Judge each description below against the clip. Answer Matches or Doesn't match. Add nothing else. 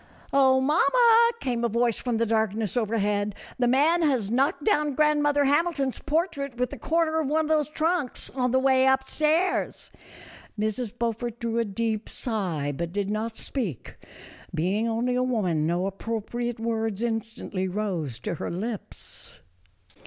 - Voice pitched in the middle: Doesn't match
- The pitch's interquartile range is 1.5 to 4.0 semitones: Doesn't match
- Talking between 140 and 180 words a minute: Matches